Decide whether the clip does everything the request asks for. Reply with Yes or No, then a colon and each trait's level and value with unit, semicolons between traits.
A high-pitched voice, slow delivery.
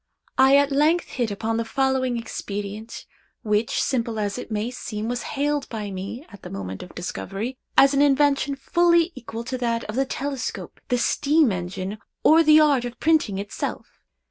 No: high, 245 Hz; average, 175 wpm